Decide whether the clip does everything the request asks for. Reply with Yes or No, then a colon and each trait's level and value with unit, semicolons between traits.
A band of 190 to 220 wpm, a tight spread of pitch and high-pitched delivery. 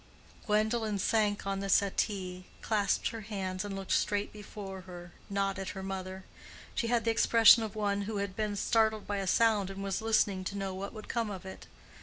Yes: average, 200 wpm; narrow, 2.0 semitones; high, 200 Hz